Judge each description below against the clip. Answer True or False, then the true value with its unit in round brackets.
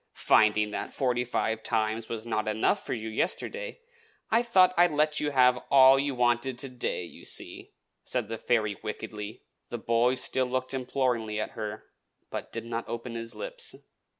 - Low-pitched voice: True (120 Hz)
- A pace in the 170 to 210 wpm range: True (180 wpm)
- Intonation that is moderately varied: True (3.2 semitones)